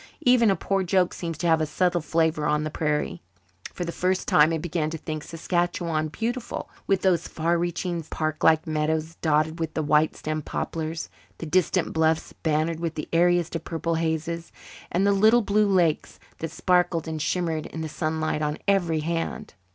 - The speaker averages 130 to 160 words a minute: No, average, 180 wpm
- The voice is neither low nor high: Yes, medium, 165 Hz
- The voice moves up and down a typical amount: No, narrow, 2.1 semitones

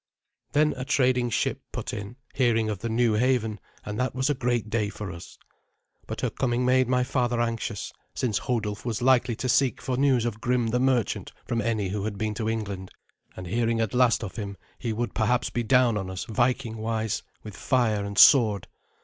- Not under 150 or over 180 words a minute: No, average, 200 wpm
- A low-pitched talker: Yes, low, 115 Hz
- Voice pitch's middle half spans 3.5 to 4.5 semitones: No, average, 2.8 semitones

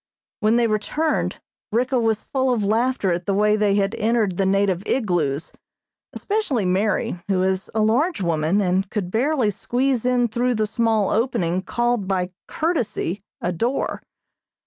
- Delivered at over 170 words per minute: No, average, 155 wpm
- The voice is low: No, high, 215 Hz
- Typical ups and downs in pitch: Yes, average, 4.2 semitones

